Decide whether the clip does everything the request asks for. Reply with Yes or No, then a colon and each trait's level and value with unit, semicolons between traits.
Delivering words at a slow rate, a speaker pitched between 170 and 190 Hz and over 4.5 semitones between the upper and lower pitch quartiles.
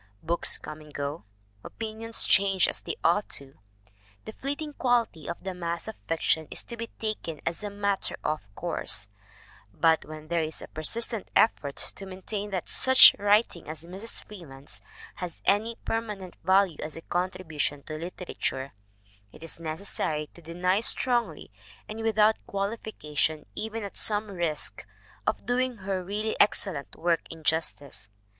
No: average, 150 wpm; medium, 185 Hz; average, 5.2 semitones